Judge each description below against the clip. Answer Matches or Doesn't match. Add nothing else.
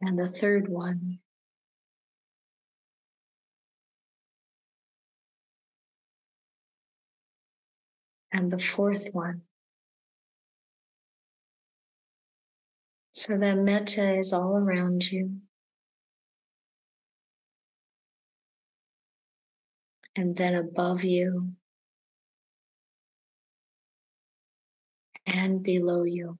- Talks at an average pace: Doesn't match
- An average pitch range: Doesn't match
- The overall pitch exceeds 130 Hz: Matches